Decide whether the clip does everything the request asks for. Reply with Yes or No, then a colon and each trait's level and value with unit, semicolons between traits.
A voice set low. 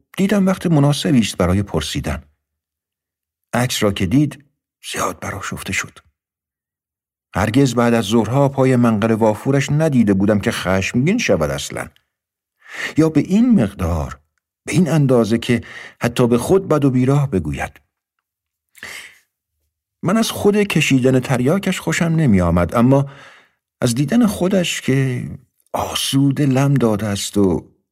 Yes: low, 120 Hz